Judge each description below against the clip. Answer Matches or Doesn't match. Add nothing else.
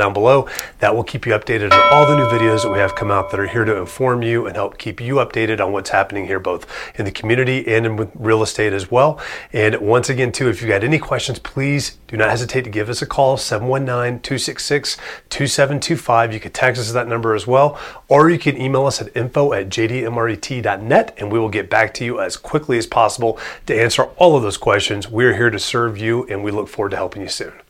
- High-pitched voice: Doesn't match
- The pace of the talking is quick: Matches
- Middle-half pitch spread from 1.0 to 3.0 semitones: Doesn't match